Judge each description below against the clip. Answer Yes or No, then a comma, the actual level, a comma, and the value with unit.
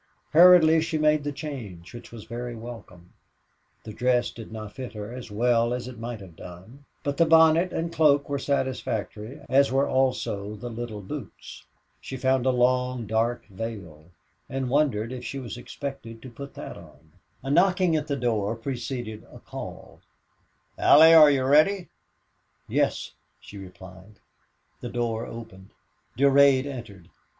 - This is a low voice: Yes, low, 125 Hz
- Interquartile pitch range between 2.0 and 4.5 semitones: Yes, average, 4.2 semitones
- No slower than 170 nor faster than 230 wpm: No, average, 155 wpm